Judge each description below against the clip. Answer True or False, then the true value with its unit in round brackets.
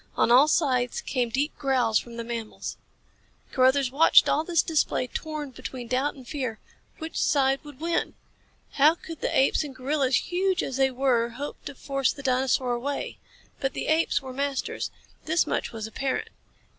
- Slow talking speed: False (170 wpm)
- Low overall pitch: False (270 Hz)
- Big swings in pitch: False (2.7 semitones)